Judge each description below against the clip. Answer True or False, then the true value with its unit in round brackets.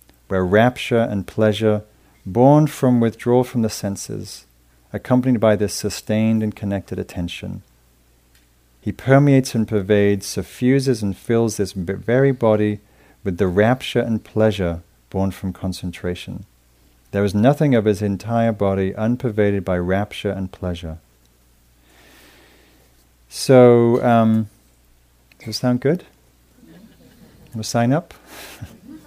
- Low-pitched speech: True (100 Hz)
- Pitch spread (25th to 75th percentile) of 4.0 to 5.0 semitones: False (5.4 semitones)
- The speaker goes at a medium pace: False (120 wpm)